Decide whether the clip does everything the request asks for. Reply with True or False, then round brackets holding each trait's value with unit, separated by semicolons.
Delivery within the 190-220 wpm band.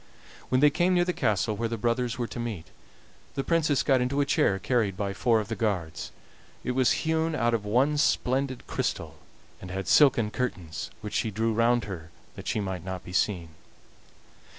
True (195 wpm)